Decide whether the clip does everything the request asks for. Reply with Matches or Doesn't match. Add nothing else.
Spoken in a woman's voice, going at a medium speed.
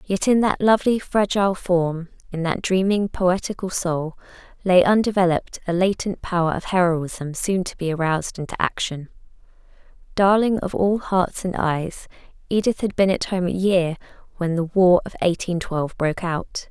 Matches